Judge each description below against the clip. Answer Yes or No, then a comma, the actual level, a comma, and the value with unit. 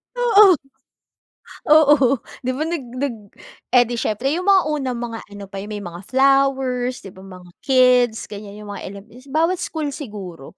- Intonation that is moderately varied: No, wide, 5.9 semitones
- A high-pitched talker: Yes, very high, 250 Hz